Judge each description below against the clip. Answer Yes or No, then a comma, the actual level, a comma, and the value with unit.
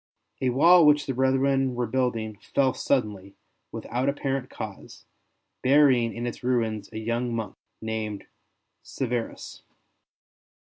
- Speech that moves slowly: Yes, slow, 115 wpm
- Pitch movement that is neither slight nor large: Yes, average, 3.1 semitones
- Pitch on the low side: Yes, low, 125 Hz